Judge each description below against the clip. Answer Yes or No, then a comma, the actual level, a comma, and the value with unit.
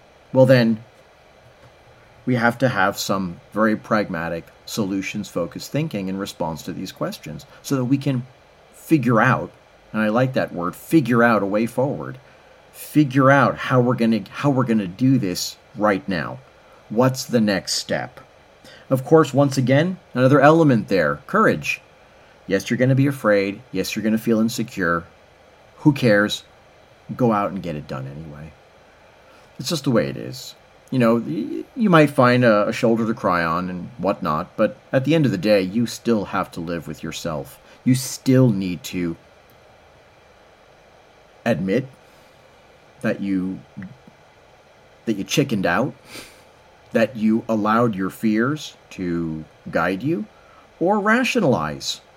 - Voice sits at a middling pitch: No, low, 120 Hz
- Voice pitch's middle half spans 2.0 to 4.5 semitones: No, average, 5.0 semitones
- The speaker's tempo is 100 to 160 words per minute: Yes, average, 155 wpm